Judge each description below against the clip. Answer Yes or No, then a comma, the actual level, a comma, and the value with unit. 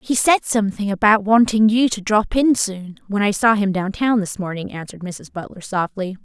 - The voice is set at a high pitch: Yes, high, 205 Hz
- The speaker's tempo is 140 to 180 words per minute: No, average, 200 wpm